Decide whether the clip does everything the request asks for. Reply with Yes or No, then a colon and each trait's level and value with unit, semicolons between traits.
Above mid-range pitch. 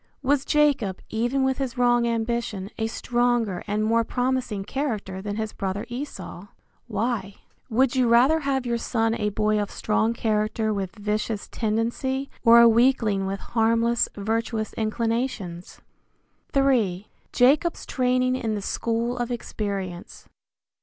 Yes: high, 230 Hz